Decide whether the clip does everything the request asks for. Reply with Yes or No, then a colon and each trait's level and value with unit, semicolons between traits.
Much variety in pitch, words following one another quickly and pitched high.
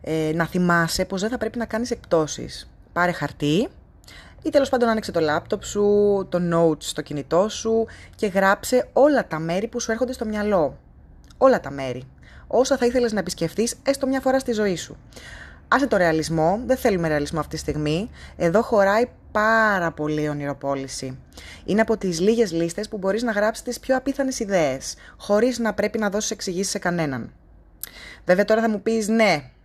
Yes: wide, 5.8 semitones; fast, 180 wpm; high, 200 Hz